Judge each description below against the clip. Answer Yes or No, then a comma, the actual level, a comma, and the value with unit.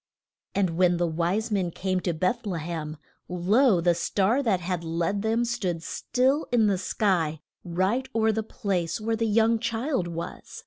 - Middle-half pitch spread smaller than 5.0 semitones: Yes, average, 4.5 semitones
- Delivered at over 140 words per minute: Yes, average, 175 wpm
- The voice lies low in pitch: No, high, 190 Hz